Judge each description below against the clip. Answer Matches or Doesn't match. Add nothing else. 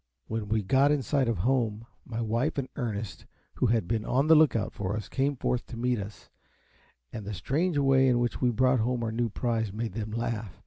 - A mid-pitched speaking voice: Doesn't match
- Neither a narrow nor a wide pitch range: Matches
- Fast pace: Matches